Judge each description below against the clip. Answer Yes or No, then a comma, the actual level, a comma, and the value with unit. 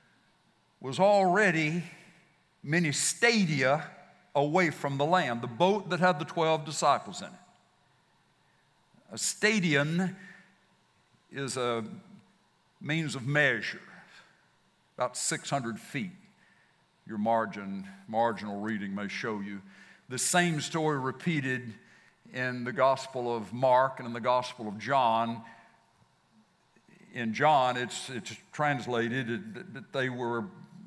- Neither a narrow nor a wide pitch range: No, wide, 6.8 semitones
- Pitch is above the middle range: No, medium, 140 Hz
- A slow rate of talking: Yes, slow, 115 wpm